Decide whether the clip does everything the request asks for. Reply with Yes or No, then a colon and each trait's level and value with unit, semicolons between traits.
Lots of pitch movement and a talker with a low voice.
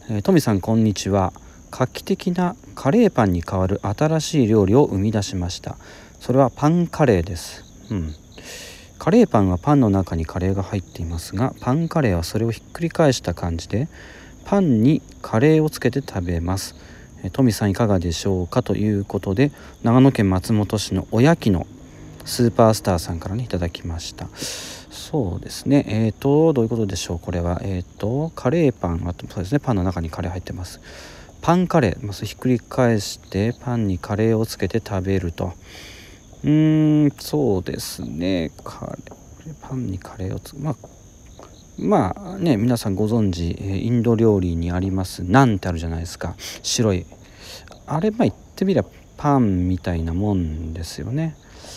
Yes: wide, 5.8 semitones; low, 105 Hz